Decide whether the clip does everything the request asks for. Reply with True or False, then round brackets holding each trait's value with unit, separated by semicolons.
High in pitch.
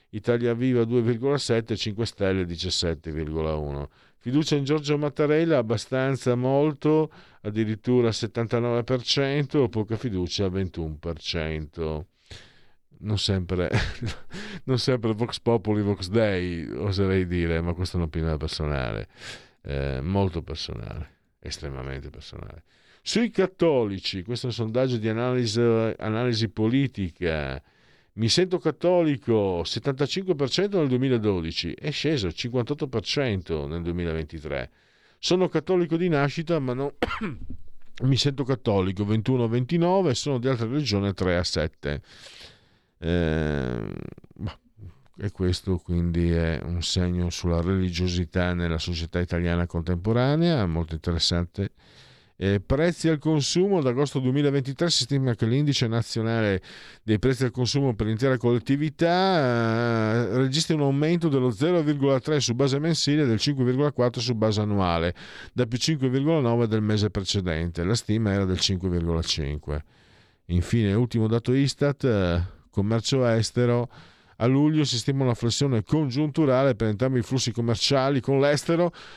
False (115 Hz)